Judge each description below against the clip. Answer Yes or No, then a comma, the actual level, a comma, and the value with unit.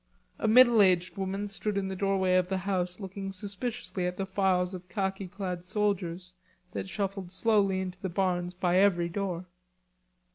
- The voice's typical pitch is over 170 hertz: Yes, high, 190 Hz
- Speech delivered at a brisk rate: No, average, 170 wpm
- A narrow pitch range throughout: Yes, narrow, 1.6 semitones